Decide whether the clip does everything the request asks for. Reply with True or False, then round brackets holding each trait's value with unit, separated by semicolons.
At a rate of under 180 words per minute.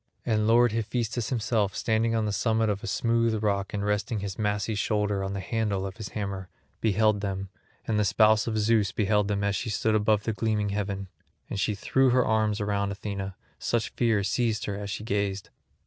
False (200 wpm)